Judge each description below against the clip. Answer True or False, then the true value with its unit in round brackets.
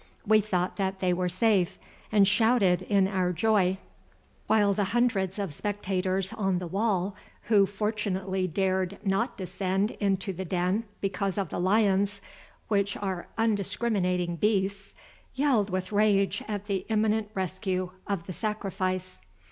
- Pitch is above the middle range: True (195 Hz)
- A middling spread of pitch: False (2.0 semitones)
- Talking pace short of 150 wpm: True (140 wpm)